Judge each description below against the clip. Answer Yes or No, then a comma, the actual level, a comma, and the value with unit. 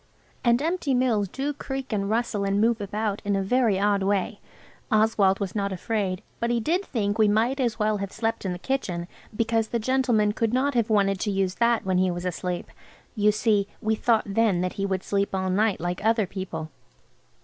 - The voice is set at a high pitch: Yes, high, 210 Hz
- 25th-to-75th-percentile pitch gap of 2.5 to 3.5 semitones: Yes, average, 3.0 semitones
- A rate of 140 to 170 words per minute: No, fast, 205 wpm